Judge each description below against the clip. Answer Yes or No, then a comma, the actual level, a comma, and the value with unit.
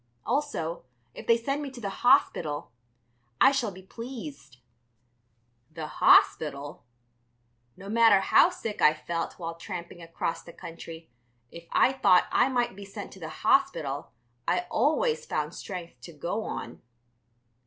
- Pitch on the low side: No, medium, 185 Hz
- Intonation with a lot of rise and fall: Yes, wide, 6.5 semitones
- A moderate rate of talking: Yes, average, 145 wpm